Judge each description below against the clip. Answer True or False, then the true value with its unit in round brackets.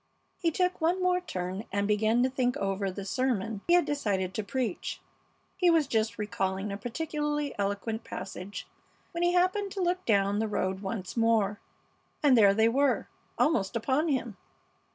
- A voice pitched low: False (225 Hz)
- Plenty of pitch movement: True (6.9 semitones)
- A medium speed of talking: True (170 wpm)